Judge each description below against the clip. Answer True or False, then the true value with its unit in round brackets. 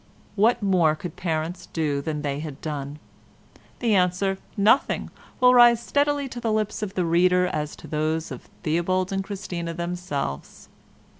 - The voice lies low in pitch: False (180 Hz)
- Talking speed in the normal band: True (160 wpm)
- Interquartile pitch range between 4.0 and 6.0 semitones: True (4.6 semitones)